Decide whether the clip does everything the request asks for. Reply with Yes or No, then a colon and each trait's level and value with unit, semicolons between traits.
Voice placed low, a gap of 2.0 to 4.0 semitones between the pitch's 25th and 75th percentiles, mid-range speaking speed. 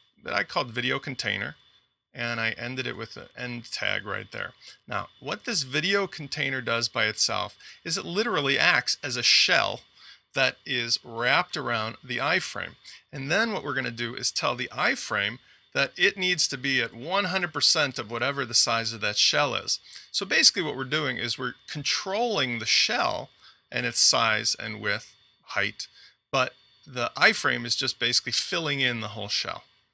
Yes: low, 125 Hz; average, 3.7 semitones; average, 180 wpm